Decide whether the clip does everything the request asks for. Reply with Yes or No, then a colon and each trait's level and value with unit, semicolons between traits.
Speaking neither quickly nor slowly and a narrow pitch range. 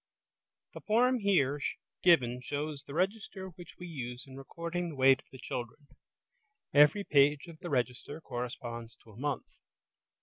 No: average, 160 wpm; average, 5.2 semitones